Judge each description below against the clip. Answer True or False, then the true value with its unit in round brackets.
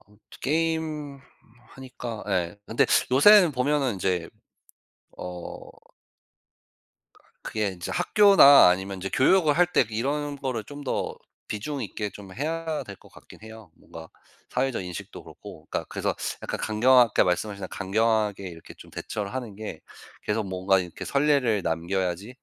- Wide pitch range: True (6.6 semitones)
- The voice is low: True (110 Hz)